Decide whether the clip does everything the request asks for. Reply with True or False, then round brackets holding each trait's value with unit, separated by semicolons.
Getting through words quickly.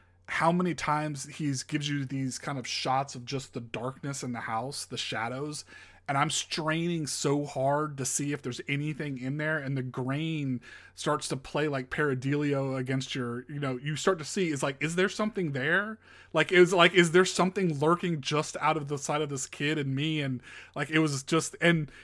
True (210 wpm)